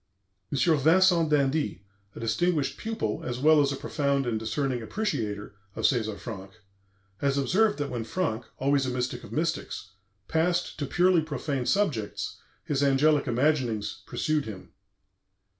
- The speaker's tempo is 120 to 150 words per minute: Yes, average, 140 wpm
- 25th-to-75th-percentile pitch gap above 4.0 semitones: Yes, average, 4.8 semitones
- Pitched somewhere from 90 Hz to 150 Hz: Yes, medium, 140 Hz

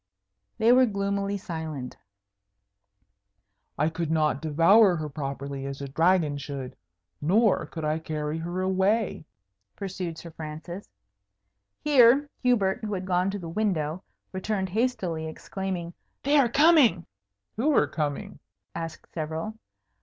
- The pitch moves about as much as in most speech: Yes, average, 4.7 semitones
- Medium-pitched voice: Yes, medium, 175 Hz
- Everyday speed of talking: No, slow, 125 wpm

